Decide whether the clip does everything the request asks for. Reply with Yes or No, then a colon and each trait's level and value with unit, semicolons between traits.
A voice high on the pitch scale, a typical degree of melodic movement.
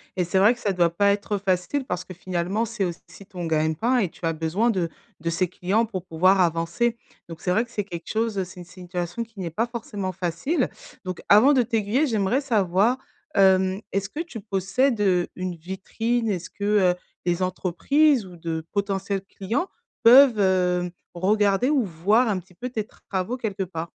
Yes: high, 195 Hz; average, 4.1 semitones